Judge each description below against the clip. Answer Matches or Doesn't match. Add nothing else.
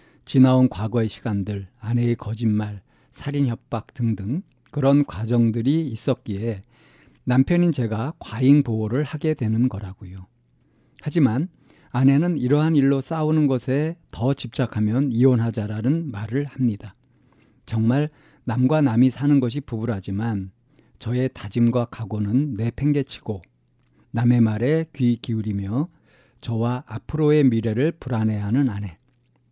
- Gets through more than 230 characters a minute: Matches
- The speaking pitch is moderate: Doesn't match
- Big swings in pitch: Doesn't match